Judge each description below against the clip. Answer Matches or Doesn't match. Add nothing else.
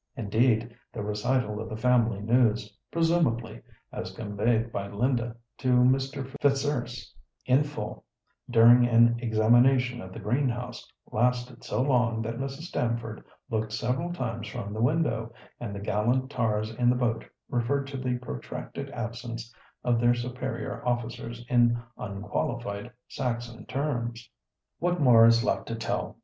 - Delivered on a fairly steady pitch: Matches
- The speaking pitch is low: Matches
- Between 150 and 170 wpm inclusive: Doesn't match